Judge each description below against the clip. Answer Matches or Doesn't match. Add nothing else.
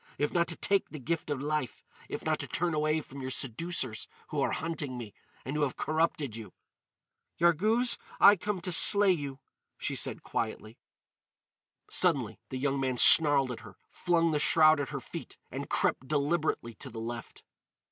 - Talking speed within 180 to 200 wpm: Doesn't match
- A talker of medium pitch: Matches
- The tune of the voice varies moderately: Matches